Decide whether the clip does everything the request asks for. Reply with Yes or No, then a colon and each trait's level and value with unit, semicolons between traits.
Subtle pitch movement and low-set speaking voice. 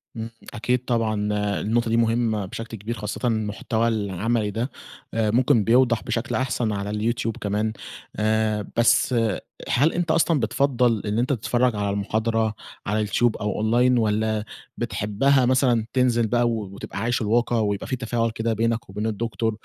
Yes: narrow, 2.2 semitones; low, 115 Hz